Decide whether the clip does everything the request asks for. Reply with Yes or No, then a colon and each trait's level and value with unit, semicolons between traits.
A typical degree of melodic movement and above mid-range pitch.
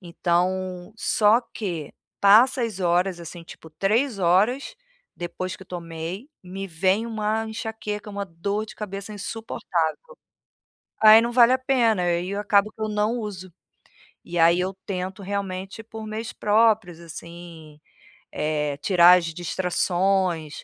Yes: average, 3.7 semitones; high, 195 Hz